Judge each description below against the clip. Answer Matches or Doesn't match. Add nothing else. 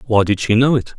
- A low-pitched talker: Matches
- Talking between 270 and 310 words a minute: Matches